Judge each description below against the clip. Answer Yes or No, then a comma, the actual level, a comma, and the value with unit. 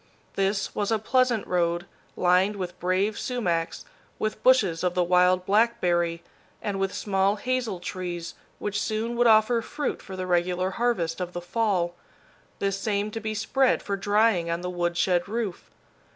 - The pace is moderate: Yes, average, 160 wpm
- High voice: Yes, high, 195 Hz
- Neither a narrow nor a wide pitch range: Yes, average, 3.5 semitones